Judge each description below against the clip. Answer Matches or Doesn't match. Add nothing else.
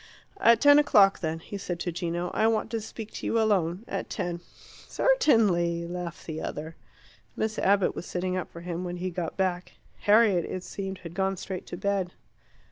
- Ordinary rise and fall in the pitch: Matches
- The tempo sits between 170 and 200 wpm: Matches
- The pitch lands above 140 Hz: Matches